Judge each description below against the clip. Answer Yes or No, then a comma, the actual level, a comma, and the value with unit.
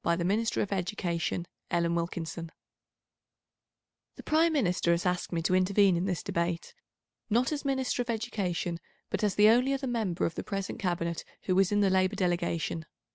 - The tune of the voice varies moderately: Yes, average, 4.1 semitones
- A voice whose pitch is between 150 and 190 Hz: Yes, medium, 185 Hz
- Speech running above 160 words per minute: Yes, average, 180 wpm